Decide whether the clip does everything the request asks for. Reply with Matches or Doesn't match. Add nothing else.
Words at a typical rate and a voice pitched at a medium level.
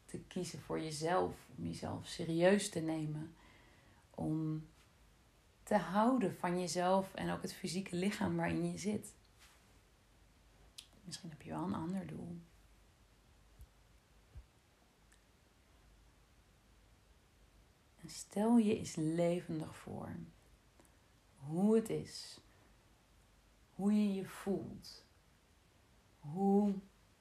Doesn't match